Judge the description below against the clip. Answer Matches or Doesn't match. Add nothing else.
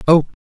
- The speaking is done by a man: Matches